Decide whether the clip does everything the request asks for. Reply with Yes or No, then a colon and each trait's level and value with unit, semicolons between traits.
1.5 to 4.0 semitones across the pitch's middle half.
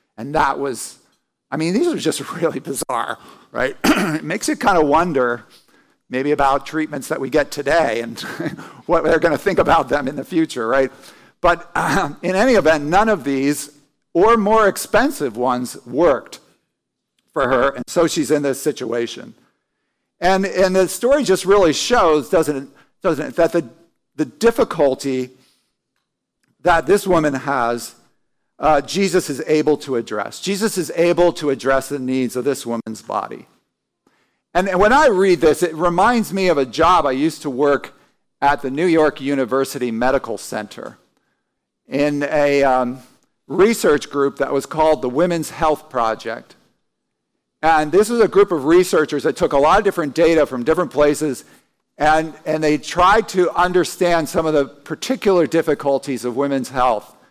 No: average, 4.5 semitones